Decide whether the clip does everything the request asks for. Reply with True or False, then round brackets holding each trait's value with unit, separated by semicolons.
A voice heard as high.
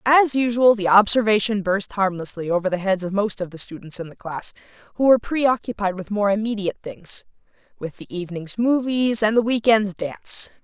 True (205 Hz)